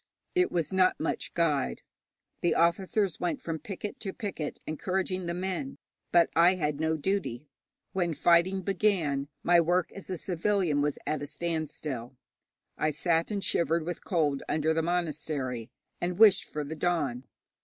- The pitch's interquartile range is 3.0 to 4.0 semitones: Yes, average, 3.4 semitones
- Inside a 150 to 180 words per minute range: Yes, average, 155 wpm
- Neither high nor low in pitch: Yes, medium, 170 Hz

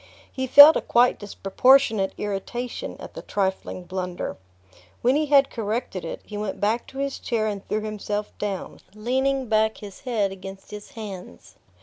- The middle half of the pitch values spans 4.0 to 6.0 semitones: Yes, average, 4.3 semitones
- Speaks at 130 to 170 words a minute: Yes, average, 160 wpm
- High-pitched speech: Yes, high, 215 Hz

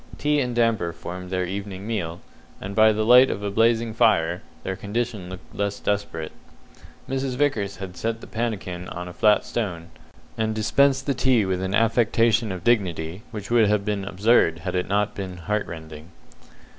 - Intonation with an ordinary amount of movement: Yes, average, 3.8 semitones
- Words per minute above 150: Yes, average, 180 wpm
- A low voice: Yes, low, 105 Hz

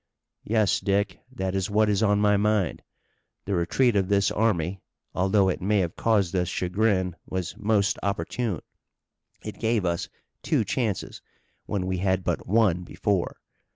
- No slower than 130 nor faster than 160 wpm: Yes, average, 155 wpm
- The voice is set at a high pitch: No, low, 100 Hz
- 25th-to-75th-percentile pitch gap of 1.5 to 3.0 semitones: Yes, narrow, 2.5 semitones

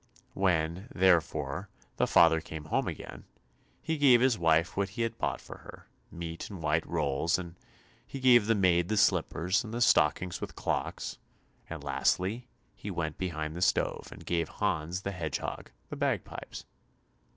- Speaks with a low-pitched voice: Yes, very low, 90 Hz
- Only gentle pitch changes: No, average, 4.1 semitones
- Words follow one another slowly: No, average, 165 wpm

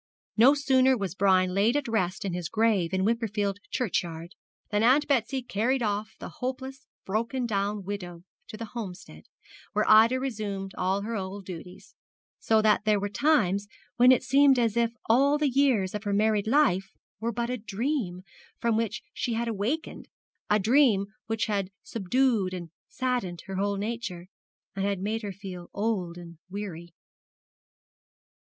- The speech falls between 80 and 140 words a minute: No, average, 160 wpm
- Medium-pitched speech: No, high, 210 Hz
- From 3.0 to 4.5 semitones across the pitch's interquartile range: Yes, average, 3.7 semitones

